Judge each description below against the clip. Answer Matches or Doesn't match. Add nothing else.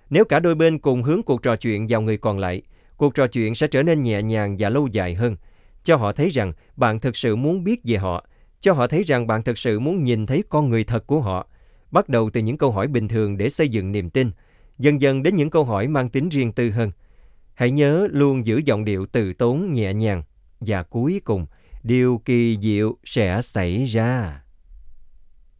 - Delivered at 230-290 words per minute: Doesn't match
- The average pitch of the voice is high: Doesn't match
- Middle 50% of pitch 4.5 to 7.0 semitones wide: Matches